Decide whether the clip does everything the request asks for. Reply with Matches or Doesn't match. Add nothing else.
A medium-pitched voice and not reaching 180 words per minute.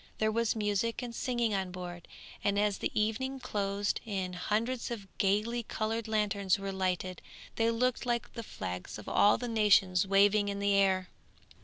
Doesn't match